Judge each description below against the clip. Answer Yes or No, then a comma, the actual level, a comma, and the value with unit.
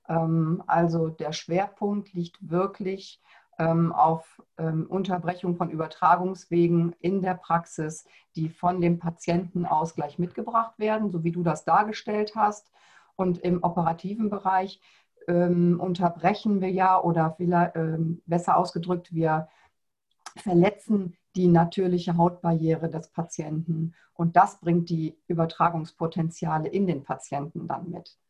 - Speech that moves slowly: Yes, slow, 110 wpm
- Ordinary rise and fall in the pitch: No, narrow, 2.0 semitones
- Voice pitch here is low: No, medium, 175 Hz